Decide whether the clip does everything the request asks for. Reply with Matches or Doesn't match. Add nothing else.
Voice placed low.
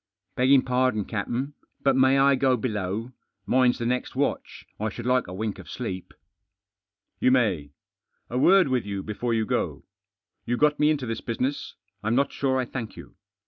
Matches